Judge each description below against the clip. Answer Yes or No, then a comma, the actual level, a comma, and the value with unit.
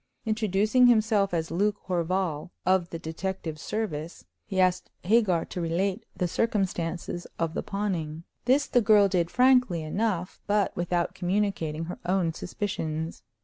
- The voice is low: No, medium, 185 Hz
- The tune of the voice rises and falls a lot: No, average, 3.8 semitones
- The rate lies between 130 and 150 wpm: Yes, average, 140 wpm